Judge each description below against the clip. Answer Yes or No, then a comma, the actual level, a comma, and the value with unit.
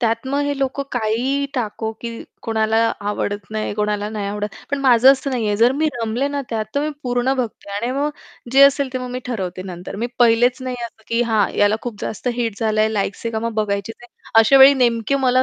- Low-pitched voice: No, high, 230 Hz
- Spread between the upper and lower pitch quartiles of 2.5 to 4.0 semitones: Yes, average, 3.2 semitones